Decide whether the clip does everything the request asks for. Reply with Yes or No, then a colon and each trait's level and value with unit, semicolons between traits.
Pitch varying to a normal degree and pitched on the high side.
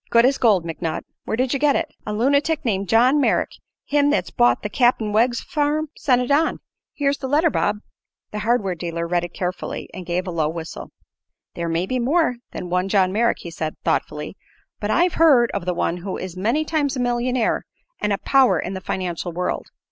No: wide, 7.1 semitones; high, 220 Hz